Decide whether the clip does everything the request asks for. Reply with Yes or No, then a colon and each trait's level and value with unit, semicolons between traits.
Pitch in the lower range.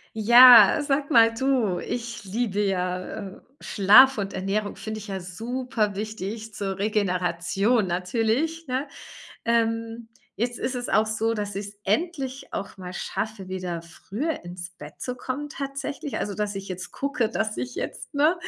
No: high, 220 Hz